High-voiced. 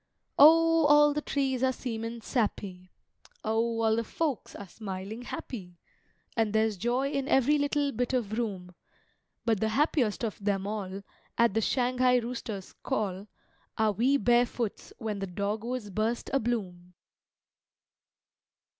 Yes: high, 230 Hz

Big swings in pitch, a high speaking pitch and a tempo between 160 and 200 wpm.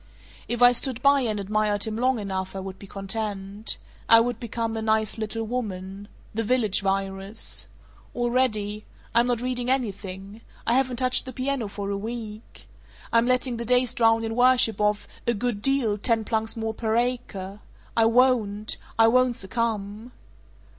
No: average, 3.0 semitones; high, 225 Hz; average, 165 wpm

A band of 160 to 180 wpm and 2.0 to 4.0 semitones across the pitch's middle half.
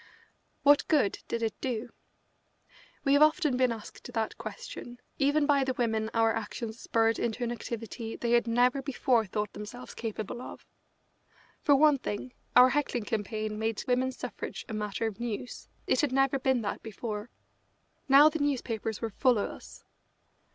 Yes: average, 165 wpm; average, 3.1 semitones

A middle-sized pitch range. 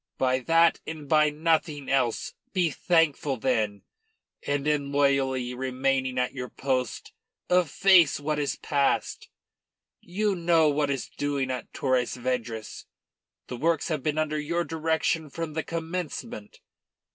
Yes: average, 3.7 semitones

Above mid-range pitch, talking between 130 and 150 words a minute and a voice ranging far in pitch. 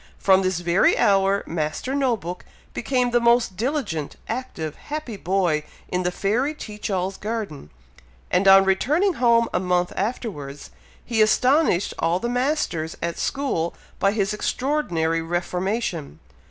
Yes: high, 195 Hz; average, 140 wpm; wide, 5.7 semitones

